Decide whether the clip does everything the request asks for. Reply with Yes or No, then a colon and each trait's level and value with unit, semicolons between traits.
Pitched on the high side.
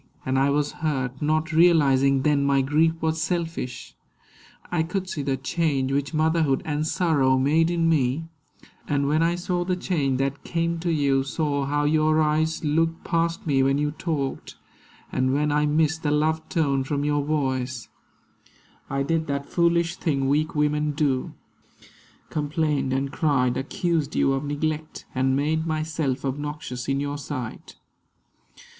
No: medium, 150 Hz